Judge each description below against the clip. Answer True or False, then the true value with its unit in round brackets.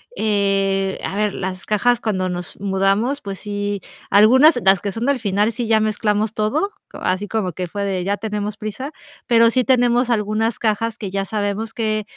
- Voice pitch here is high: True (210 Hz)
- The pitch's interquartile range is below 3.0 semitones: True (2.4 semitones)